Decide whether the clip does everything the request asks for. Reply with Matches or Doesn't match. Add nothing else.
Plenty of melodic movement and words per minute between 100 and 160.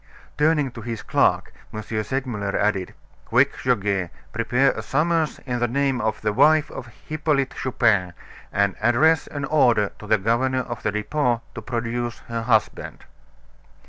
Doesn't match